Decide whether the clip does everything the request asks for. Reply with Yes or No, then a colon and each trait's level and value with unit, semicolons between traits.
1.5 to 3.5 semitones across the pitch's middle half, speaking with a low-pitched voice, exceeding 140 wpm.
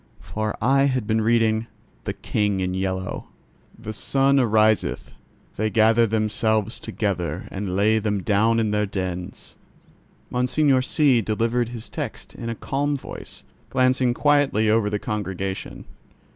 No: average, 3.0 semitones; low, 110 Hz; slow, 135 wpm